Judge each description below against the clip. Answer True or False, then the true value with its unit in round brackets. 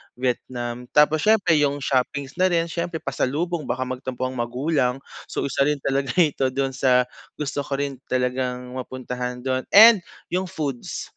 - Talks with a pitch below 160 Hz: True (135 Hz)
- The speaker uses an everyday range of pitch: True (3.1 semitones)